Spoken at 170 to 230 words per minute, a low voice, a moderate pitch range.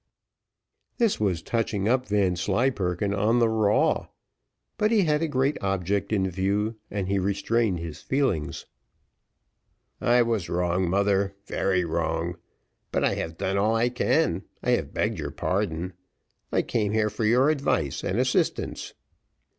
No: average, 145 wpm; low, 100 Hz; average, 4.1 semitones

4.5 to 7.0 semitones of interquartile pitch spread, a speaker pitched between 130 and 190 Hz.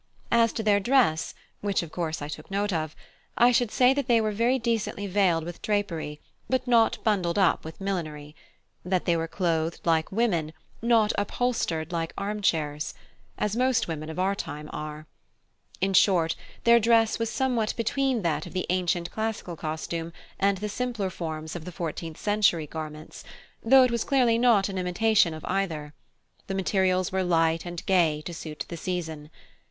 Yes: average, 5.2 semitones; medium, 185 Hz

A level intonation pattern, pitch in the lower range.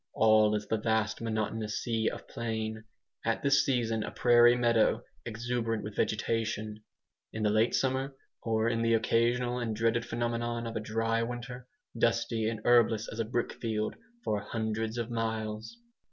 Yes: narrow, 1.3 semitones; low, 115 Hz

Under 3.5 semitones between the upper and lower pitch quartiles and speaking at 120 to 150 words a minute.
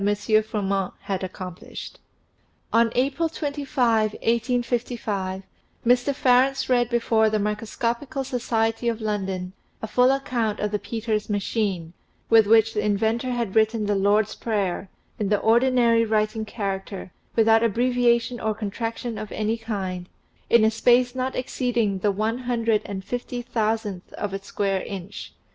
Yes: average, 2.8 semitones; average, 140 wpm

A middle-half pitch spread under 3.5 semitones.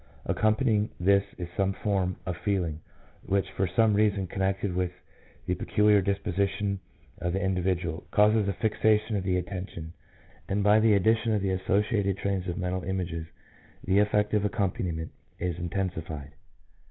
Yes: narrow, 2.4 semitones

